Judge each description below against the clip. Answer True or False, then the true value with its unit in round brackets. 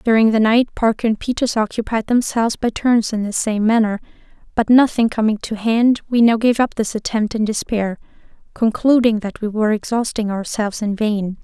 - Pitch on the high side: True (220 Hz)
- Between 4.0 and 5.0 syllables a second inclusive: False (5.3 syllables/s)